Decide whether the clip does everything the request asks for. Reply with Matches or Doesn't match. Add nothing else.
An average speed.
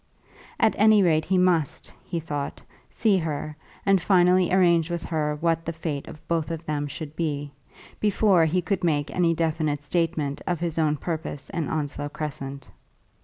Matches